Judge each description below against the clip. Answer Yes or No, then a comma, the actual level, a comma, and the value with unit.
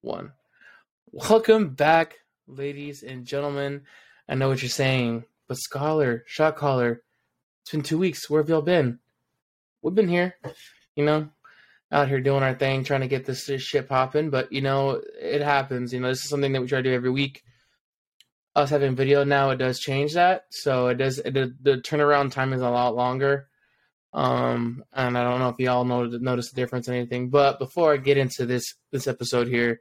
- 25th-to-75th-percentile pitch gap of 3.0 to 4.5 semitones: No, narrow, 2.5 semitones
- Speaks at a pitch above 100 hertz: Yes, low, 135 Hz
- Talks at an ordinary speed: Yes, average, 195 wpm